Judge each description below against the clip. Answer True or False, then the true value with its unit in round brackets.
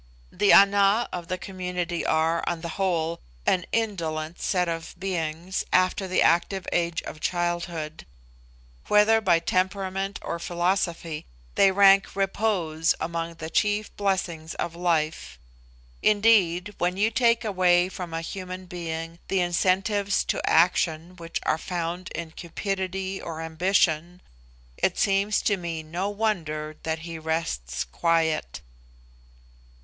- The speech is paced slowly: True (130 wpm)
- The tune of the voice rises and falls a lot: False (2.8 semitones)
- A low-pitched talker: False (175 Hz)